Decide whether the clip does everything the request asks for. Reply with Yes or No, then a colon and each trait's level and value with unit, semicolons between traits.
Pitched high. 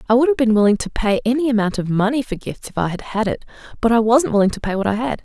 Yes: high, 225 Hz